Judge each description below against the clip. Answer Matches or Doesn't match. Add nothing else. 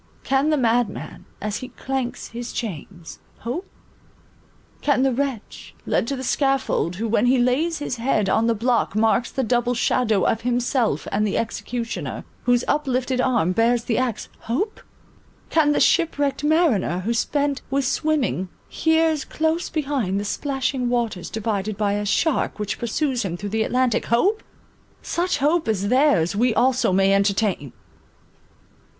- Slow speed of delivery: Doesn't match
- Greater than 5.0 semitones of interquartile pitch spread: Doesn't match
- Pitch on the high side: Matches